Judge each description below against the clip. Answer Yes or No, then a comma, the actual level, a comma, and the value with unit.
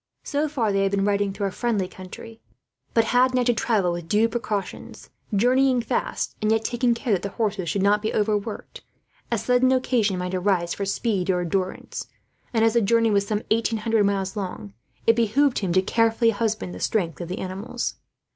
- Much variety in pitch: No, average, 3.1 semitones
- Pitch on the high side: Yes, high, 215 Hz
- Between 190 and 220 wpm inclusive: Yes, average, 200 wpm